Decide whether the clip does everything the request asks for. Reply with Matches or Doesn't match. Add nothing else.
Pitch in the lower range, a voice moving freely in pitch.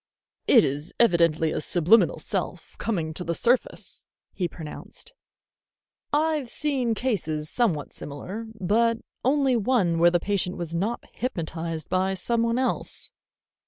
Doesn't match